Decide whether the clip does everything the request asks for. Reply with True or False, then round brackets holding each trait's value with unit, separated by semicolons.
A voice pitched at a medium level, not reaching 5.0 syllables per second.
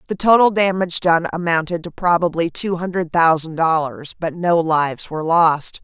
False (170 Hz; 5.1 syllables/s)